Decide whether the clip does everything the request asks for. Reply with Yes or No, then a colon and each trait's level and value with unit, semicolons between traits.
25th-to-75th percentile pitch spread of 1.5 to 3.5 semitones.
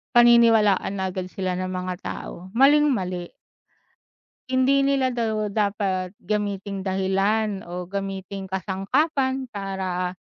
No: average, 3.9 semitones